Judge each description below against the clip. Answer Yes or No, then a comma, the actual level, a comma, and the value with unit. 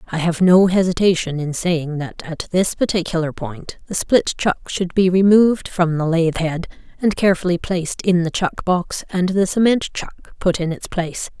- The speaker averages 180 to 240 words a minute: Yes, average, 190 wpm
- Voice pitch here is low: No, medium, 175 Hz